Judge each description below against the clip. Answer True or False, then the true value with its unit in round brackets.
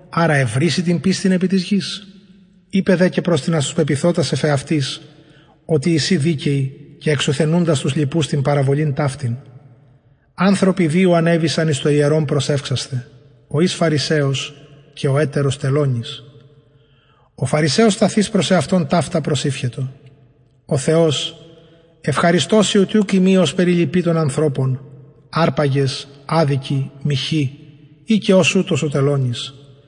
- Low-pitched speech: False (155 Hz)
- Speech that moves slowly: True (120 wpm)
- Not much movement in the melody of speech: False (3.4 semitones)